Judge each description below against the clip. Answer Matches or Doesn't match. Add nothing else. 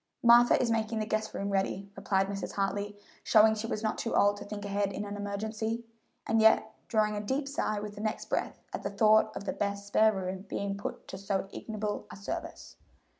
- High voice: Matches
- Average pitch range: Doesn't match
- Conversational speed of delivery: Doesn't match